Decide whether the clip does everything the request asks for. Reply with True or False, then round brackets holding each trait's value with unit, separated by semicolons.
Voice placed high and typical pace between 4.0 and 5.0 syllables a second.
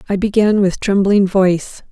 True (195 Hz; 4.8 syllables/s)